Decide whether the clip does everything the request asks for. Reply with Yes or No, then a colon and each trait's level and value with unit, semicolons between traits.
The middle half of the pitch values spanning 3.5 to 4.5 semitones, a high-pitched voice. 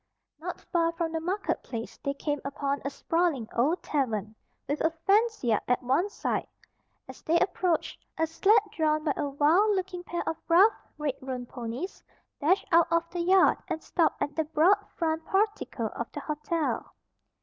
Yes: average, 4.1 semitones; very high, 320 Hz